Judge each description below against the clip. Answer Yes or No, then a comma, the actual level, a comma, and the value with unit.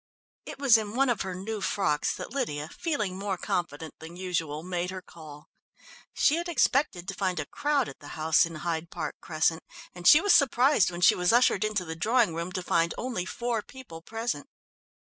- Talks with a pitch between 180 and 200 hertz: Yes, medium, 185 Hz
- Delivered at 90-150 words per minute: No, average, 195 wpm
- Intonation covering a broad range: Yes, wide, 6.2 semitones